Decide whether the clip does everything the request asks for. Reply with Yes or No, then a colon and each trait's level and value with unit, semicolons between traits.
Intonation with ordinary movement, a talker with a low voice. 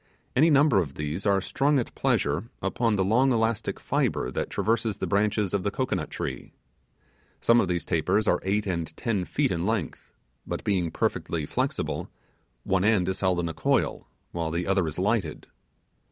Yes: average, 4.5 semitones; very low, 95 Hz